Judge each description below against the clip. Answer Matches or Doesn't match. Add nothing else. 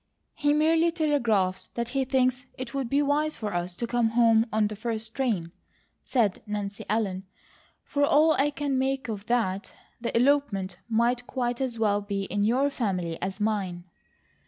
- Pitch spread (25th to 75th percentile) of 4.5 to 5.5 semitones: Matches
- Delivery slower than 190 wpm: Matches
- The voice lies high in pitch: Matches